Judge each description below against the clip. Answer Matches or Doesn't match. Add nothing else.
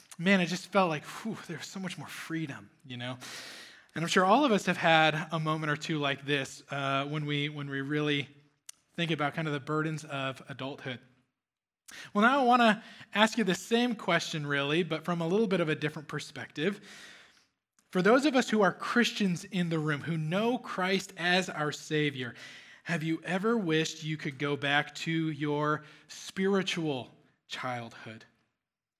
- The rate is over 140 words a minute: Matches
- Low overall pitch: Doesn't match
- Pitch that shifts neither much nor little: Matches